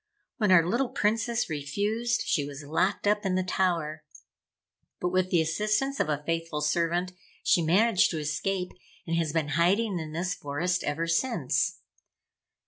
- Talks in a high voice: No, medium, 175 Hz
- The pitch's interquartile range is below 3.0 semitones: No, average, 4.5 semitones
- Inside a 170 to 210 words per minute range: No, average, 155 wpm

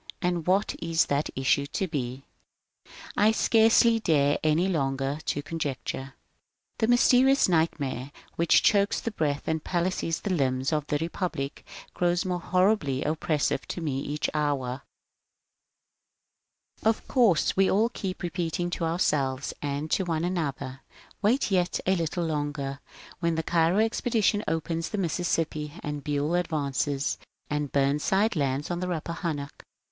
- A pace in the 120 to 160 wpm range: Yes, average, 140 wpm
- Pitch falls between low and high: Yes, medium, 160 Hz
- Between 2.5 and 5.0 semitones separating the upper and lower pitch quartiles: Yes, average, 4.2 semitones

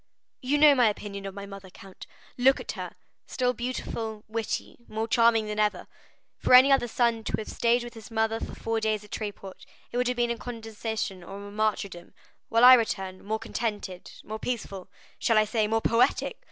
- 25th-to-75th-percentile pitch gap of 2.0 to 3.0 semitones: Yes, narrow, 2.5 semitones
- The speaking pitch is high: Yes, high, 220 Hz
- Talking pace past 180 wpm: Yes, average, 190 wpm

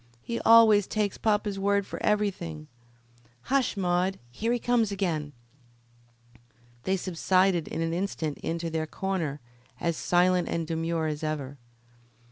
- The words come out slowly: Yes, slow, 130 wpm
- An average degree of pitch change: Yes, average, 3.9 semitones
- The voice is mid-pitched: Yes, medium, 180 Hz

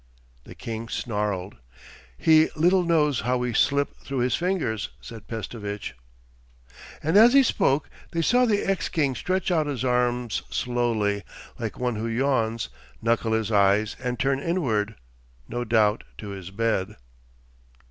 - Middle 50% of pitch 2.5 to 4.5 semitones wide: No, average, 5.3 semitones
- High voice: No, low, 120 Hz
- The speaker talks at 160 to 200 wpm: No, average, 140 wpm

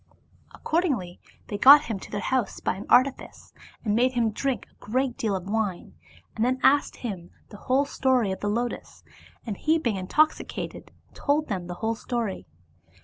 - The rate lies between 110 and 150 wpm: No, average, 170 wpm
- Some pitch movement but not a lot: Yes, average, 4.6 semitones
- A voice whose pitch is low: No, high, 230 Hz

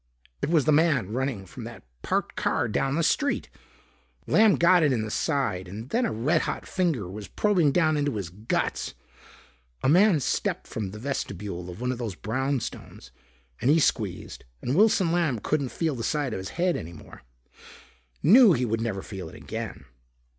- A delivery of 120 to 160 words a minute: No, average, 185 wpm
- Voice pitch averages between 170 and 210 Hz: No, low, 130 Hz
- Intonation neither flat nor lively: No, wide, 7.4 semitones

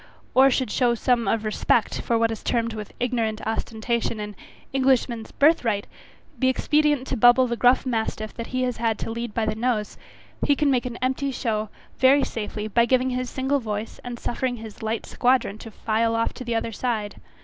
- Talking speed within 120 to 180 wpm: No, average, 195 wpm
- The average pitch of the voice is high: Yes, high, 235 Hz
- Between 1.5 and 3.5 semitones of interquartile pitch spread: Yes, narrow, 2.5 semitones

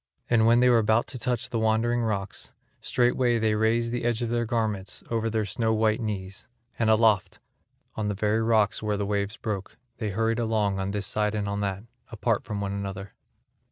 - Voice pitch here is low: Yes, low, 110 Hz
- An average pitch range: No, narrow, 2.1 semitones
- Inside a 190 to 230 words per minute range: Yes, fast, 205 wpm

